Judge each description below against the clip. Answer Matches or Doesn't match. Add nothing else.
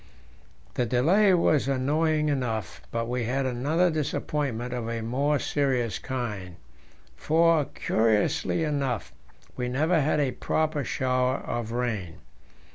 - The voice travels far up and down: Doesn't match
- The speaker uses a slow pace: Matches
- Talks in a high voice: Doesn't match